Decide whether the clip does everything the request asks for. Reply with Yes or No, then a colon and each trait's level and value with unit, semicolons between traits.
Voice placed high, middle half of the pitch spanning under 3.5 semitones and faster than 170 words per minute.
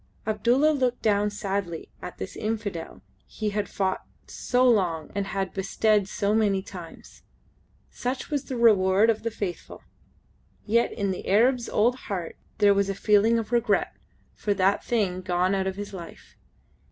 No: high, 205 Hz; average, 3.0 semitones; average, 160 wpm